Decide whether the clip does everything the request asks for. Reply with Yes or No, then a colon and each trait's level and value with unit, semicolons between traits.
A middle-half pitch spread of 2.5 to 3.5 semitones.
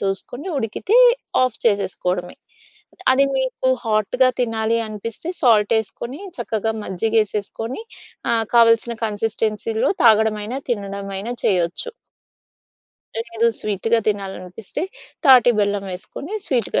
Yes: average, 2.8 semitones